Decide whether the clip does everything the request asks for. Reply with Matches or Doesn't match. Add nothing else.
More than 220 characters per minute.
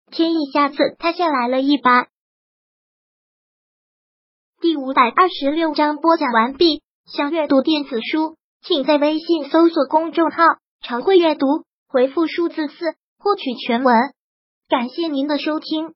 Doesn't match